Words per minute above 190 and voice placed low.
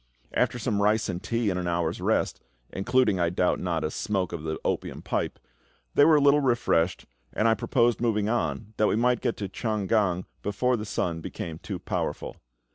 Yes: average, 200 wpm; low, 105 Hz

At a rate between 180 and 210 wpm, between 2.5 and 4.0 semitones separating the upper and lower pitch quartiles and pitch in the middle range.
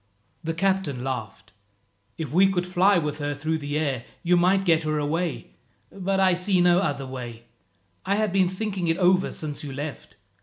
No: average, 185 wpm; average, 4.4 semitones; medium, 165 Hz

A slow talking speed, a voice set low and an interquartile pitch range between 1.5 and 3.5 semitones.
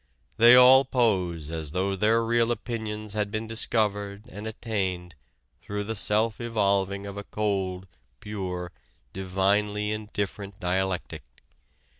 Yes: slow, 120 wpm; low, 105 Hz; narrow, 2.5 semitones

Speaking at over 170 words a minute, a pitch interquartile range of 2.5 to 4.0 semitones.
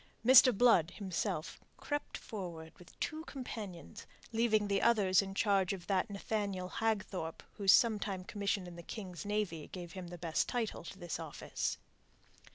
No: average, 160 wpm; average, 3.4 semitones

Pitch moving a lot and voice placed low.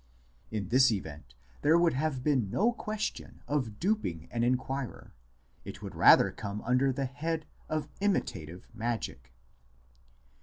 Yes: wide, 6.7 semitones; low, 130 Hz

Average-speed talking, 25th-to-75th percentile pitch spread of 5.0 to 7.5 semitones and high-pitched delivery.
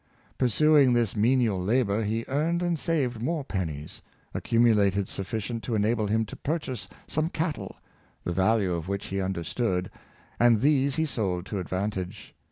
No: average, 155 wpm; average, 5.3 semitones; low, 110 Hz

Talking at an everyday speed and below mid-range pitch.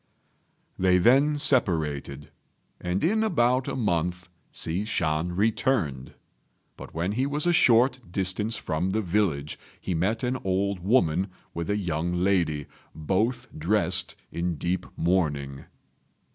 No: slow, 130 wpm; very low, 95 Hz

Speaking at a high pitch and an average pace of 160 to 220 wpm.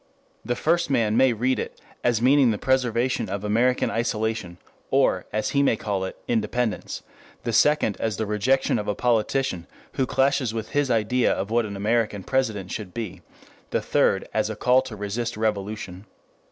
No: low, 115 Hz; average, 175 wpm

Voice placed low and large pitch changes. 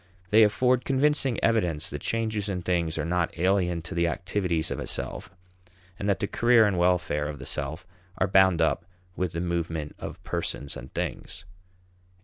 No: very low, 90 Hz; average, 3.8 semitones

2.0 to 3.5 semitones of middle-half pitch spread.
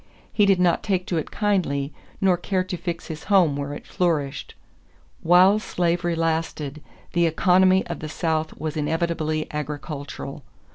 Yes: average, 2.9 semitones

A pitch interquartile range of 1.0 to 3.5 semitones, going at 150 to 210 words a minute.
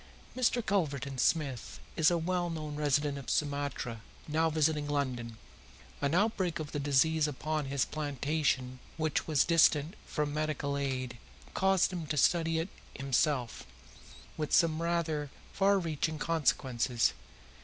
No: average, 2.8 semitones; slow, 135 wpm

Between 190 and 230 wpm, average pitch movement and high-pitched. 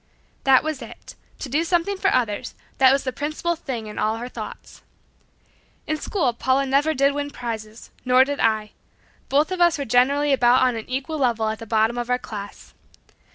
Yes: average, 195 wpm; average, 3.9 semitones; very high, 260 Hz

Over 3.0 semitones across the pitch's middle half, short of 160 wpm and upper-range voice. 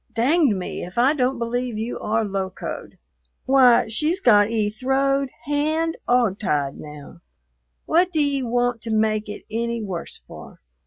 Yes: average, 4.4 semitones; average, 150 wpm; high, 235 Hz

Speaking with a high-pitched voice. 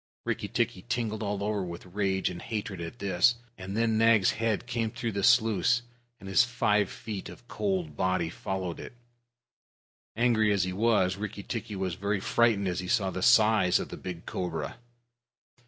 No: low, 105 Hz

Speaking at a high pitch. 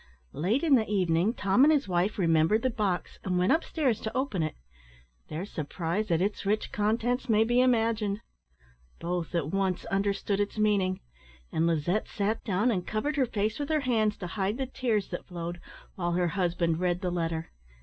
Yes: high, 200 Hz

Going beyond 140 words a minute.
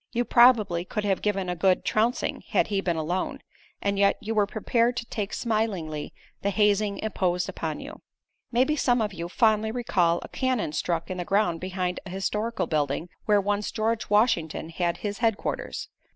Yes: average, 180 wpm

